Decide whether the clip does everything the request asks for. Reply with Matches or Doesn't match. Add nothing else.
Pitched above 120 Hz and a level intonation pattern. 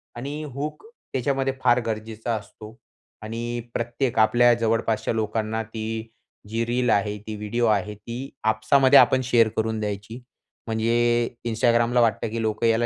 Doesn't match